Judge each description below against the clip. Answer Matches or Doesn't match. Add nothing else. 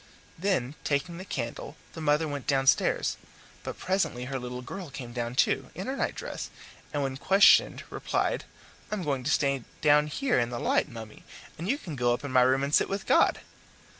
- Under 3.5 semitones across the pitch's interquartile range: Doesn't match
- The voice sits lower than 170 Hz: Matches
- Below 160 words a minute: Doesn't match